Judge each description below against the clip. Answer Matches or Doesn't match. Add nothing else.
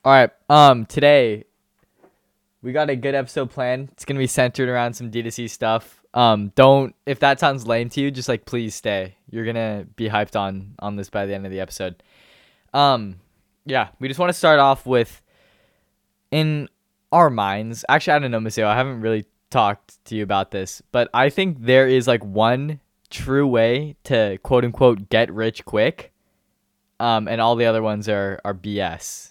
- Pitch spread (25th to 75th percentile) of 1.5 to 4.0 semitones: Doesn't match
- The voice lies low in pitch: Matches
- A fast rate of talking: Doesn't match